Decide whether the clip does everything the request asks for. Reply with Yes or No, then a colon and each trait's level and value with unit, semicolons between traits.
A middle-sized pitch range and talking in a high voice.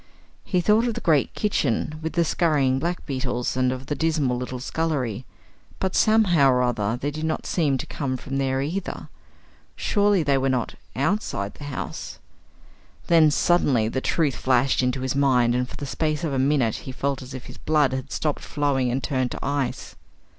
No: average, 3.5 semitones; medium, 140 Hz